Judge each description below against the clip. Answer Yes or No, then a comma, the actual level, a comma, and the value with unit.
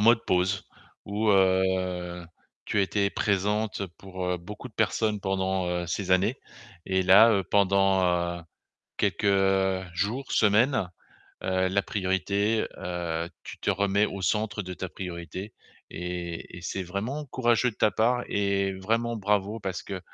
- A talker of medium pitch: No, very low, 95 Hz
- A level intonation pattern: Yes, narrow, 2.2 semitones